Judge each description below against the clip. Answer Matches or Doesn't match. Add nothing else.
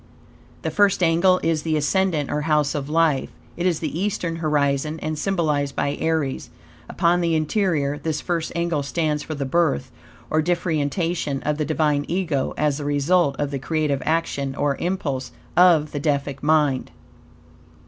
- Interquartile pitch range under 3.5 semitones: Matches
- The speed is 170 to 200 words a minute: Doesn't match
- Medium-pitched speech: Matches